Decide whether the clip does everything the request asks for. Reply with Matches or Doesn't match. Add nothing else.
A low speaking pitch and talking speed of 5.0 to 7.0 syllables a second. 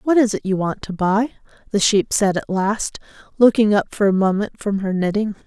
Doesn't match